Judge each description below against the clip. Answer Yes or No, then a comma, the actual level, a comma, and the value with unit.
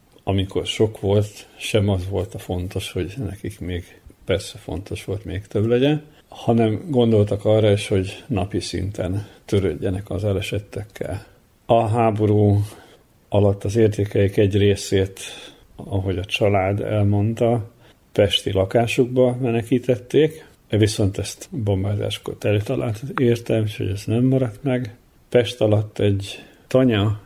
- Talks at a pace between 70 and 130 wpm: Yes, average, 125 wpm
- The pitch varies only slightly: No, average, 3.0 semitones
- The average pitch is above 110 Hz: No, low, 105 Hz